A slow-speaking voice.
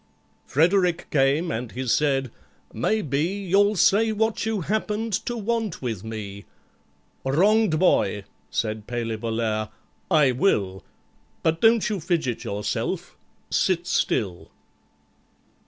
Yes: slow, 105 wpm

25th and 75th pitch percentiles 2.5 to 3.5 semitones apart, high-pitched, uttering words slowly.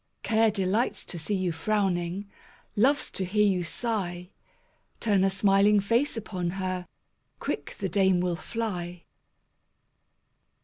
Yes: average, 2.9 semitones; high, 195 Hz; slow, 125 wpm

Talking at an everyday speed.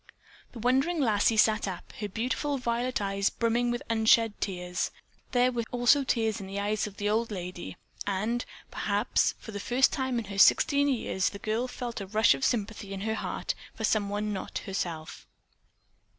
Yes: average, 180 wpm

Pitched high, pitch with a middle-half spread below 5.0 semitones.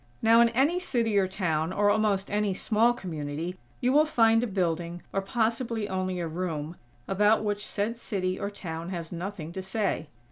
Yes: high, 195 Hz; average, 4.2 semitones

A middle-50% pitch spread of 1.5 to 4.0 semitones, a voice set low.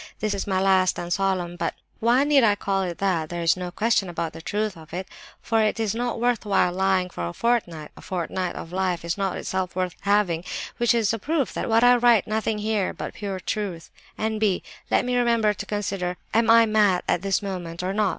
No: average, 3.4 semitones; high, 195 Hz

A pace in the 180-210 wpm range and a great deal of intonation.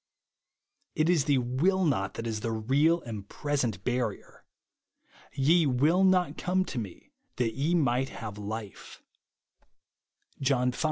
No: slow, 135 wpm; wide, 5.7 semitones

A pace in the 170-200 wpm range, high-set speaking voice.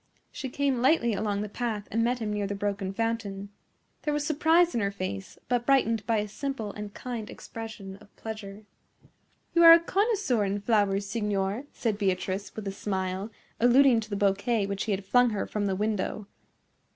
Yes: average, 190 wpm; high, 210 Hz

